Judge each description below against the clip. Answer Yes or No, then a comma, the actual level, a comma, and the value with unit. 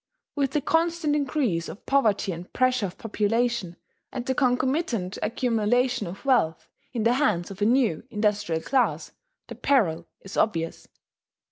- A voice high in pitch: Yes, high, 230 Hz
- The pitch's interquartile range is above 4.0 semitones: Yes, average, 5.1 semitones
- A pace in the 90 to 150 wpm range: Yes, average, 145 wpm